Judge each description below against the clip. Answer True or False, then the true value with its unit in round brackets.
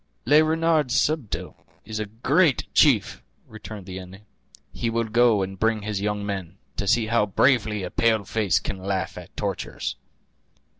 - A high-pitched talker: False (110 Hz)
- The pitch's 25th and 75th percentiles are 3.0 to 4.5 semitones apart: True (3.4 semitones)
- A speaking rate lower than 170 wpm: True (160 wpm)